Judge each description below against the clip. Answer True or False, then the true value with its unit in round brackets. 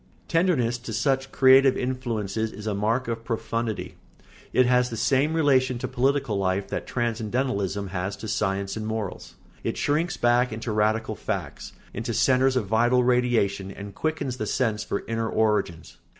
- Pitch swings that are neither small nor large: True (3.4 semitones)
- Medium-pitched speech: False (115 Hz)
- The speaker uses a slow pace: False (165 wpm)